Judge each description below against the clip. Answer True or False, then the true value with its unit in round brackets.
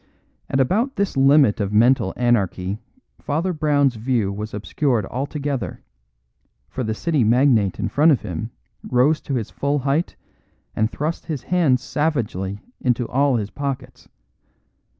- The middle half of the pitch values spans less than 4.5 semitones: False (4.8 semitones)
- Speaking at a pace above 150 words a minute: False (140 wpm)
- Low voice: True (130 Hz)